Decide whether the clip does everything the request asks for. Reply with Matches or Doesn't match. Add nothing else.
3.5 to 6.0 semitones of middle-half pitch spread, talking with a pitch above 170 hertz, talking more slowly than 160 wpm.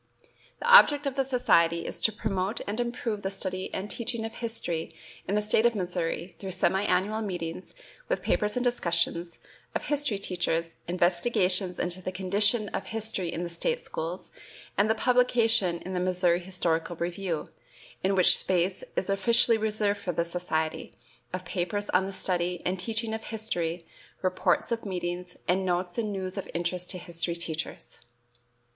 Doesn't match